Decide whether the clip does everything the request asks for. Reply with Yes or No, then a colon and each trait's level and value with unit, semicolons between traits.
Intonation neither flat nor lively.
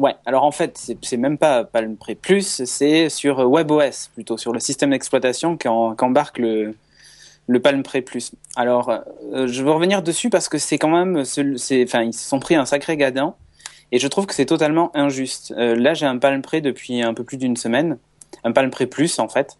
Yes: average, 3.8 semitones